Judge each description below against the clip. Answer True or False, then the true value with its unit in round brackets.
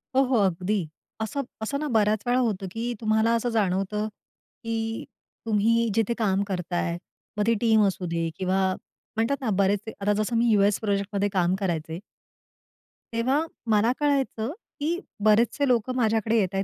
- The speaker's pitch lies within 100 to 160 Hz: False (215 Hz)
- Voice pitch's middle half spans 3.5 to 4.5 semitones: False (2.9 semitones)